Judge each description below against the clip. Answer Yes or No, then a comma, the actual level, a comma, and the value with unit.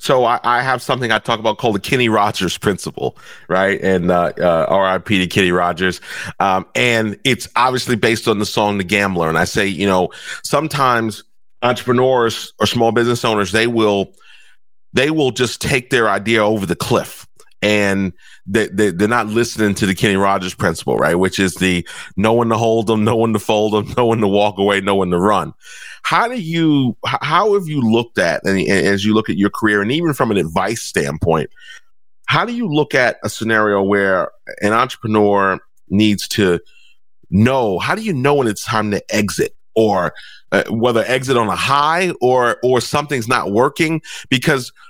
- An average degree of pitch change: Yes, average, 3.6 semitones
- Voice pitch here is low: Yes, low, 110 Hz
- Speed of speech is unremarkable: Yes, average, 190 wpm